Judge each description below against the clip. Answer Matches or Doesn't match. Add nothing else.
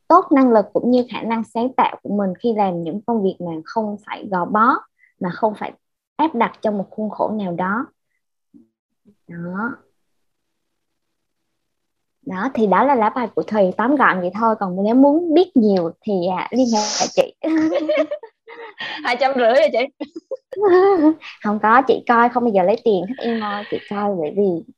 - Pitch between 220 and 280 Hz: Matches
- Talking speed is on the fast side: Doesn't match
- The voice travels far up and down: Matches